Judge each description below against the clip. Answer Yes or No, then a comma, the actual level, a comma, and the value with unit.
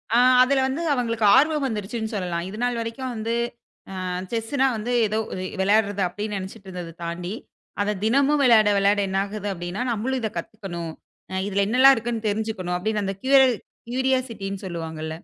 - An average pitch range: Yes, average, 4.0 semitones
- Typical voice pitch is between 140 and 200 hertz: No, high, 215 Hz